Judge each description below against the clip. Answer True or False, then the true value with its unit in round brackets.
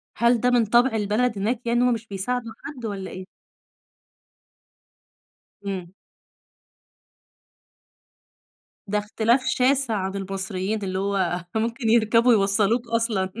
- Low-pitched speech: False (220 Hz)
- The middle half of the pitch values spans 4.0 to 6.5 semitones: False (3.4 semitones)